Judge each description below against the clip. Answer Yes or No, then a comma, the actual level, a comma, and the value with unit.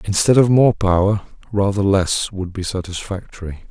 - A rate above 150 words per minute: No, average, 145 wpm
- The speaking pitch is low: Yes, low, 100 Hz